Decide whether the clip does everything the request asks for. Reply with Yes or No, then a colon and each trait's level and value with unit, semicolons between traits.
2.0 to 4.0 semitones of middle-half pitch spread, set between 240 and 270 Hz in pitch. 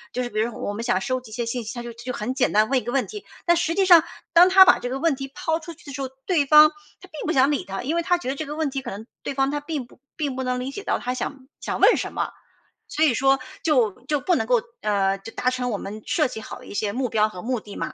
No: average, 4.5 semitones; very high, 260 Hz